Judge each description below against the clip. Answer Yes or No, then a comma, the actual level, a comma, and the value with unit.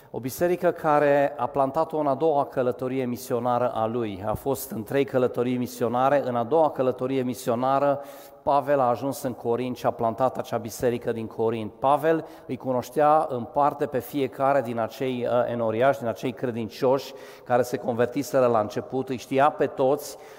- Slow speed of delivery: No, fast, 170 wpm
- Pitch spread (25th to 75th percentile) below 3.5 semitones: Yes, narrow, 2.5 semitones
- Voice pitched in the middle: No, low, 130 Hz